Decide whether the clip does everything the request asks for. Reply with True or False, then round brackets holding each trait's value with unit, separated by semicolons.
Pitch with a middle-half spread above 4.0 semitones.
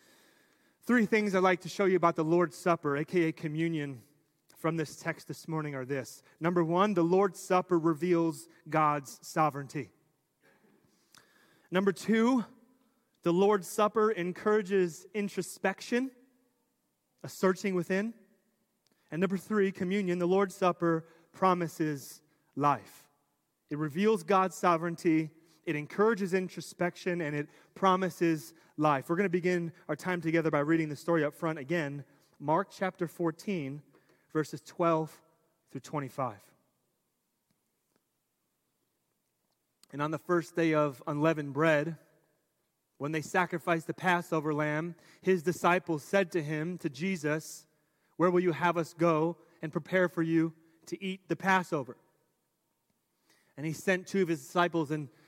False (3.2 semitones)